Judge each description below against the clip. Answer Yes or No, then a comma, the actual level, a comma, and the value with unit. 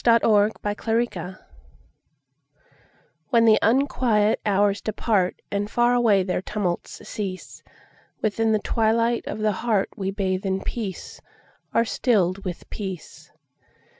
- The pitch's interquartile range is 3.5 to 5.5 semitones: No, average, 2.9 semitones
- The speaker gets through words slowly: Yes, slow, 110 wpm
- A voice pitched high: Yes, high, 210 Hz